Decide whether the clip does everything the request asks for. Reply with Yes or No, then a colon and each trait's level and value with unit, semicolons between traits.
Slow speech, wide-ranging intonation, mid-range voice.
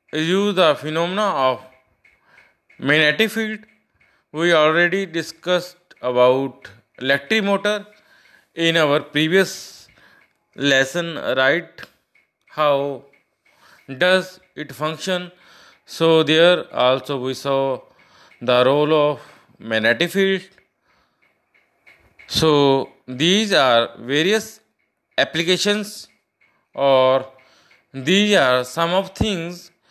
Yes: slow, 85 wpm; wide, 5.8 semitones; medium, 160 Hz